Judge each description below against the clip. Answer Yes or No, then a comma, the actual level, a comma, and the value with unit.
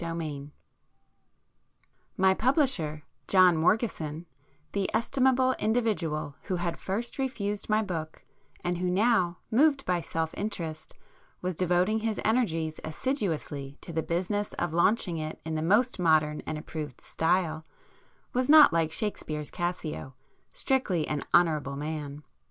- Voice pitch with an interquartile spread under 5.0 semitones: No, wide, 5.4 semitones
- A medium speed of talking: No, slow, 130 wpm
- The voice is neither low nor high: Yes, medium, 175 Hz